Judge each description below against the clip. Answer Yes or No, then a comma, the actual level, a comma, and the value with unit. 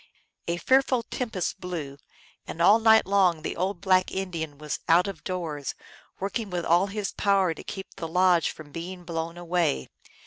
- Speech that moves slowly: No, average, 170 wpm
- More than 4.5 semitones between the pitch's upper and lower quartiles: No, average, 2.9 semitones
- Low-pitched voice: No, medium, 180 Hz